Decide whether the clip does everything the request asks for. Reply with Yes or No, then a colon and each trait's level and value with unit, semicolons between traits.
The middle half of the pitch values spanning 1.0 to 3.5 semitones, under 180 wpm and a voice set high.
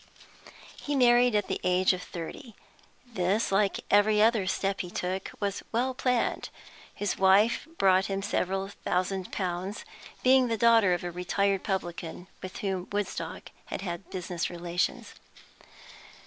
Yes: average, 2.9 semitones; average, 140 wpm; high, 195 Hz